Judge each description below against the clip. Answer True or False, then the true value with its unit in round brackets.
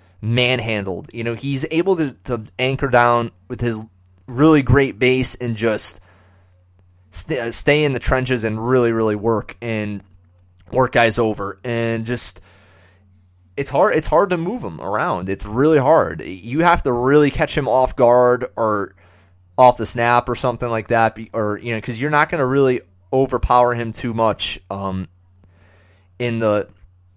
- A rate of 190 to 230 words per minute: False (165 wpm)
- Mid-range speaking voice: False (115 Hz)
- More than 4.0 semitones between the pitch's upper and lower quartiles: True (5.0 semitones)